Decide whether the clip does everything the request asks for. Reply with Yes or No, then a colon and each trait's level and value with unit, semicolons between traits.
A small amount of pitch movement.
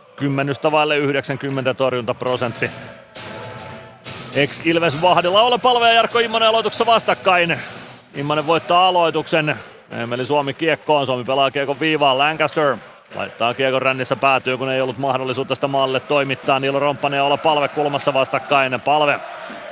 No: average, 3.1 semitones